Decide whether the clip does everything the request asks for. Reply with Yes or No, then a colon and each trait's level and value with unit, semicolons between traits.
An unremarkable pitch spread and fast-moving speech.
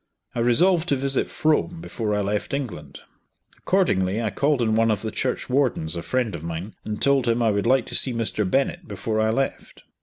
Yes: average, 4.7 semitones; fast, 210 wpm